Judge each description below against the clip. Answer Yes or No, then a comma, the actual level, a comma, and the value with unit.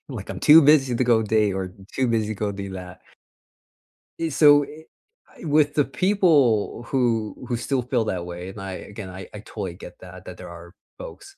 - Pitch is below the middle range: Yes, low, 115 Hz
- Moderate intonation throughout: No, wide, 7.0 semitones